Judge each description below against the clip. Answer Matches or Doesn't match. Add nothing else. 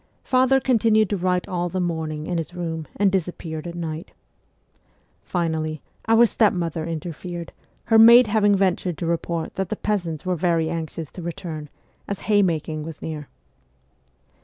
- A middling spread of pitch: Matches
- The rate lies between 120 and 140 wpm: Doesn't match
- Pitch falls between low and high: Matches